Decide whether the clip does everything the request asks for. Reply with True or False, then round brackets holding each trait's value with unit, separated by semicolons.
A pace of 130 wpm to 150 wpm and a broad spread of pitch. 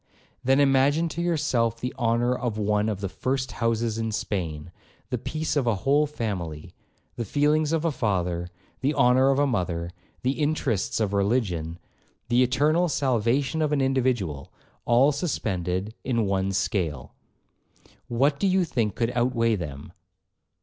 True (140 wpm; 5.9 semitones)